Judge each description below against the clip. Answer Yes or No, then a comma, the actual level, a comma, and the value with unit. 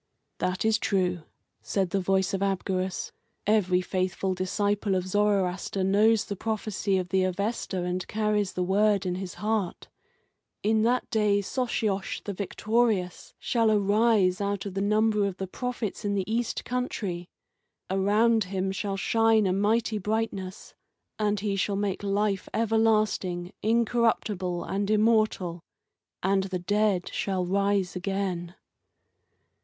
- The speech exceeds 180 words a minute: No, slow, 135 wpm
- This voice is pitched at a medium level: No, high, 200 Hz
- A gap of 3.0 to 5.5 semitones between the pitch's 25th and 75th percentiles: No, narrow, 2.4 semitones